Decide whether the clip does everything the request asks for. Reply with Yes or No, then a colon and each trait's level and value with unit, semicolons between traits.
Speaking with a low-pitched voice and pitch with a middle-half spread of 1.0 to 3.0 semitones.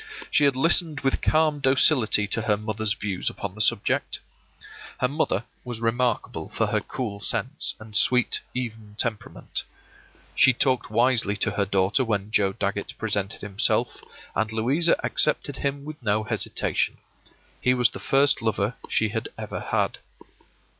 No: low, 115 Hz; average, 4.2 semitones